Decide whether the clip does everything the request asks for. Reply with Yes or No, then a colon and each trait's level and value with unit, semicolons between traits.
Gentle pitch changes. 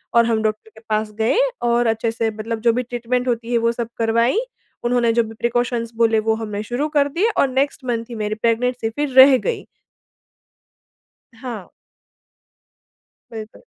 Yes: narrow, 1.8 semitones